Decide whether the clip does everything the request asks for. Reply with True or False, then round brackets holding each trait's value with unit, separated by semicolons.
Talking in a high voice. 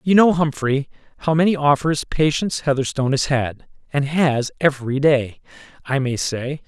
False (140 Hz)